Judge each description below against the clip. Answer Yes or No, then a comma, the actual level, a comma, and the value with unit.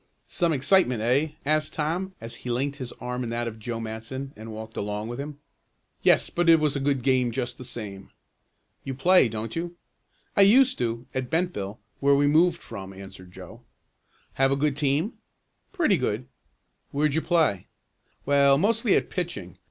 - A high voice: No, low, 135 Hz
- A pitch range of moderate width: No, wide, 5.7 semitones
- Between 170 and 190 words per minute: Yes, average, 175 wpm